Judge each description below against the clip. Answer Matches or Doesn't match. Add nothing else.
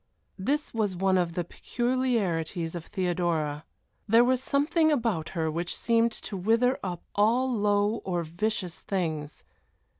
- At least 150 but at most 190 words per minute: Doesn't match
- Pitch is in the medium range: Doesn't match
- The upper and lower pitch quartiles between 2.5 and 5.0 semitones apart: Doesn't match